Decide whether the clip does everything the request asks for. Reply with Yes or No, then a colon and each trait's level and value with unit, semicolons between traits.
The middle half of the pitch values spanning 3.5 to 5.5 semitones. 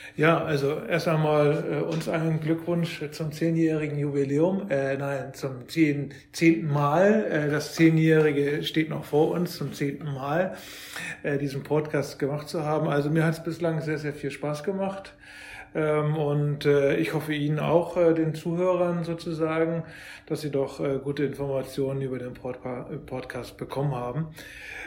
No: narrow, 2.5 semitones